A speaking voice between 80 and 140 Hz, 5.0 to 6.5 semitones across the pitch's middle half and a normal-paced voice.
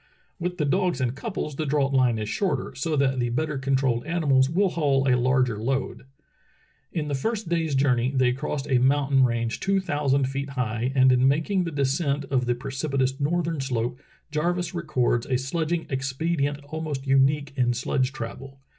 No: low, 135 Hz; average, 3.1 semitones; average, 180 wpm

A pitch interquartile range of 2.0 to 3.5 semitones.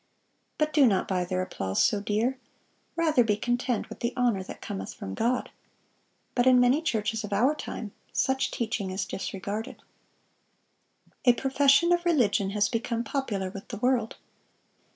No: average, 4.4 semitones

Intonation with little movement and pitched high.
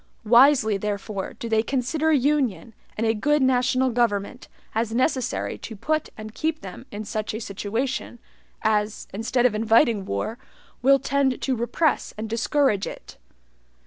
No: average, 3.7 semitones; high, 230 Hz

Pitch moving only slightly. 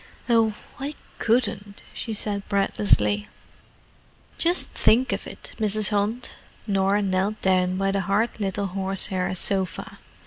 Yes: narrow, 2.0 semitones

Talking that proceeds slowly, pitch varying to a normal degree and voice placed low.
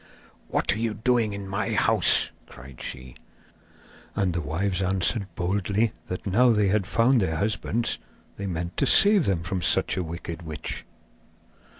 No: average, 160 wpm; average, 4.0 semitones; very low, 95 Hz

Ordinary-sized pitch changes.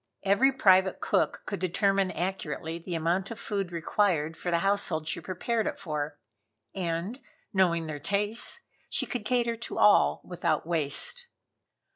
Yes: average, 3.7 semitones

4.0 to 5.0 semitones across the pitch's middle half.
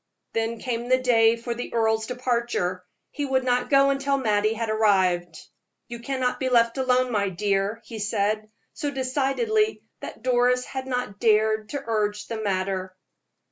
No: average, 3.3 semitones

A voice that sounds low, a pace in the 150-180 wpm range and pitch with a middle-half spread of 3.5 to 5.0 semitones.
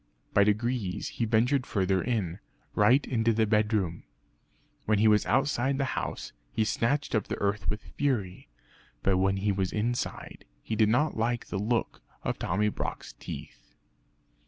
No: low, 110 Hz; average, 160 wpm; average, 3.1 semitones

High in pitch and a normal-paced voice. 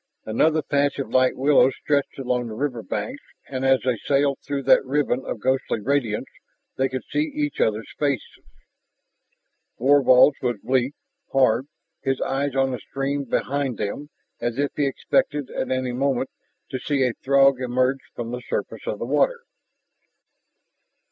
No: low, 135 Hz; average, 155 wpm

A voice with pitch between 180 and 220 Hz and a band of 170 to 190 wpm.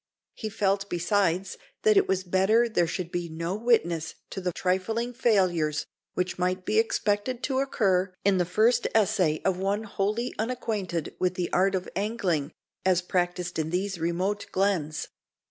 No: high, 190 Hz; average, 160 wpm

